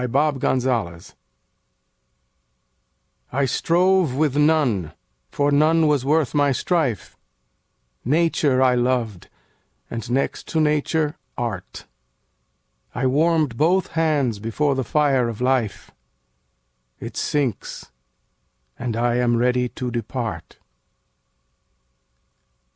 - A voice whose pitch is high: No, low, 130 Hz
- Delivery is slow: Yes, slow, 100 wpm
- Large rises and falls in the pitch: No, average, 4.1 semitones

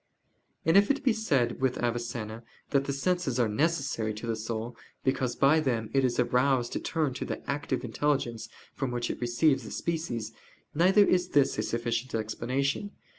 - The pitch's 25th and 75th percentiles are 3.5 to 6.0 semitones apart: Yes, average, 3.9 semitones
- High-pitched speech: No, low, 130 Hz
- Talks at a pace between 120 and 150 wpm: No, average, 175 wpm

